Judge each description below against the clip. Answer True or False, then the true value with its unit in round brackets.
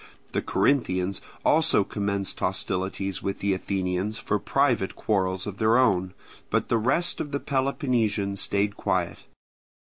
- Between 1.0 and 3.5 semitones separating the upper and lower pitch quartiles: False (4.1 semitones)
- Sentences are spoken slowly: True (130 wpm)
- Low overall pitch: True (100 Hz)